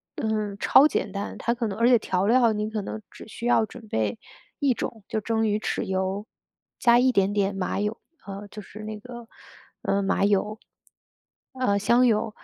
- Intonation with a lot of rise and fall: No, average, 2.8 semitones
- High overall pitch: Yes, high, 215 Hz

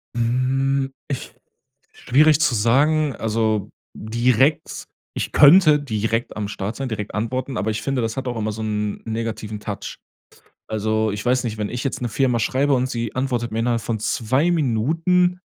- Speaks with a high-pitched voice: No, low, 120 Hz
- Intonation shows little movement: No, average, 3.7 semitones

